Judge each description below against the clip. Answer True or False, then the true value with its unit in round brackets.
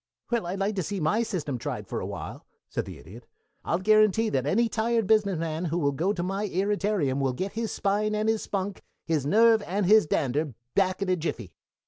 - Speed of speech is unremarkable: False (215 wpm)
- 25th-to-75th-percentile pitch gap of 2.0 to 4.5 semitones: False (5.2 semitones)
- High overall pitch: True (195 Hz)